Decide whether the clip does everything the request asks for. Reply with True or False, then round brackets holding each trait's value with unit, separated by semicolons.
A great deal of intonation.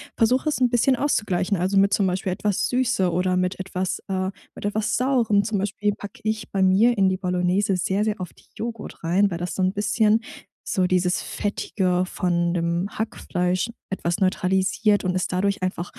False (2.6 semitones)